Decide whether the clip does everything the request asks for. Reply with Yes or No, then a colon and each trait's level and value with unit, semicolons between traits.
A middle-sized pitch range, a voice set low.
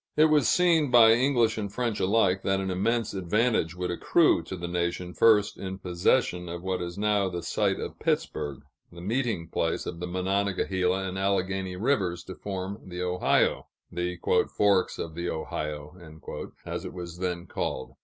Yes: average, 3.0 semitones; very low, 95 Hz